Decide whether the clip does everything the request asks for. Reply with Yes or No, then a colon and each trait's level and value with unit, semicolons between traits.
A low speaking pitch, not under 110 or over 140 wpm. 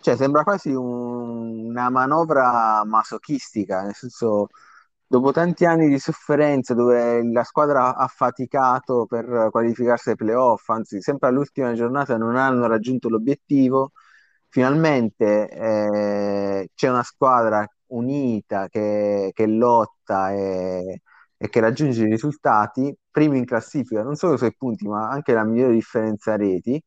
Yes: low, 120 Hz; average, 135 wpm